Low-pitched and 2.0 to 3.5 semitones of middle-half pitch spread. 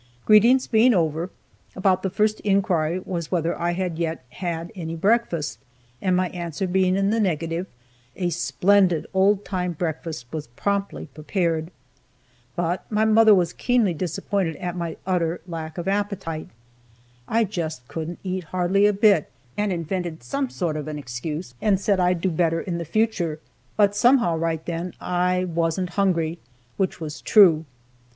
No: medium, 180 Hz; average, 3.1 semitones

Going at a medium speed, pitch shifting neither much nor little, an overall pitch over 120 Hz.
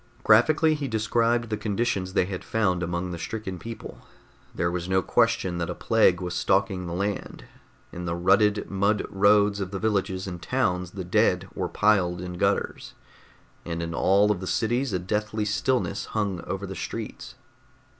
No: average, 175 wpm; average, 3.1 semitones; very low, 95 Hz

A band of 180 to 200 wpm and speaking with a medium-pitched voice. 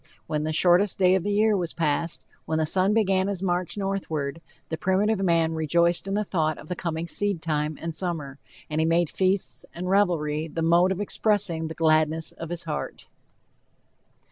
Yes: average, 185 wpm; medium, 170 Hz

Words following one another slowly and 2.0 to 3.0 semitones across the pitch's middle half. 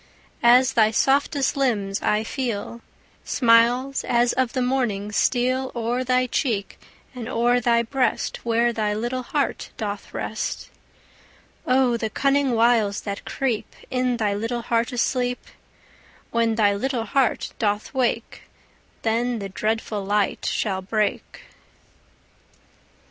Yes: slow, 125 wpm; average, 2.7 semitones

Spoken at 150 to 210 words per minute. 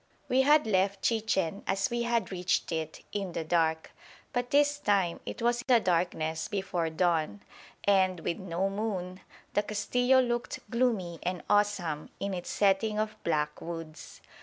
Yes: average, 155 wpm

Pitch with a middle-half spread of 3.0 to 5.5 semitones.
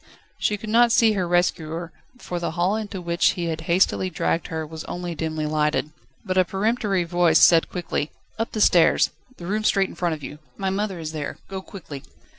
Yes: average, 3.3 semitones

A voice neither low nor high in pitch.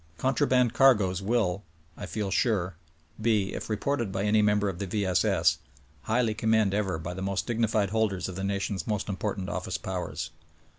No: low, 105 Hz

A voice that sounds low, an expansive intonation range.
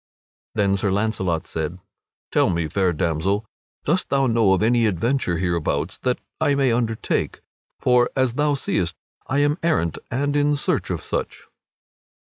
Yes: low, 110 Hz; wide, 7.2 semitones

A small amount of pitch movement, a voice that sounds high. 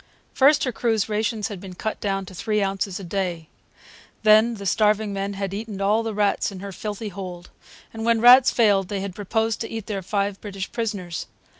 Yes: narrow, 2.2 semitones; high, 205 Hz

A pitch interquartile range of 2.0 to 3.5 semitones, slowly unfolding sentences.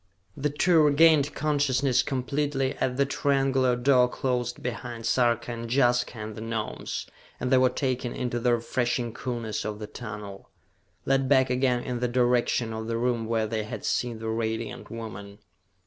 No: narrow, 2.5 semitones; average, 165 wpm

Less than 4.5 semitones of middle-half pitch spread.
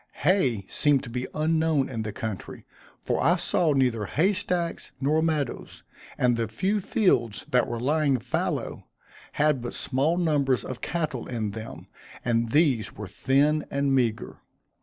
No: average, 5.0 semitones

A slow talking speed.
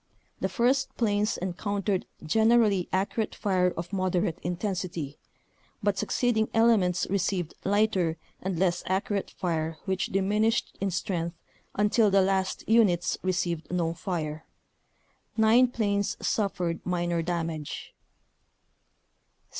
Yes: slow, 110 wpm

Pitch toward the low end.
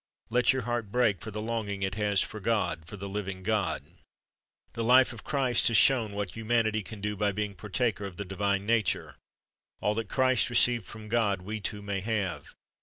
Yes: low, 105 Hz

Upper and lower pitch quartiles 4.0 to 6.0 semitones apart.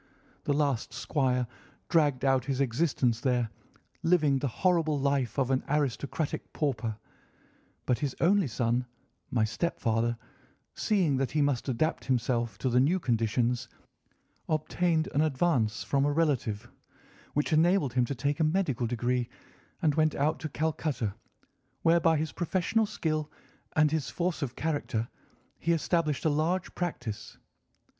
Yes: average, 4.4 semitones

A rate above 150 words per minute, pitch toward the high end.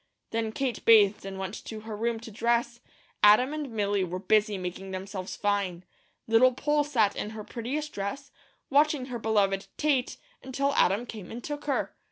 Yes: average, 175 wpm; high, 225 Hz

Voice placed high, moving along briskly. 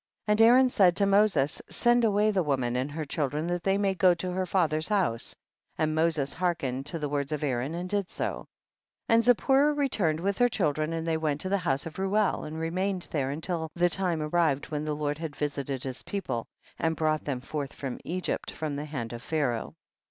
No: medium, 160 Hz; fast, 220 wpm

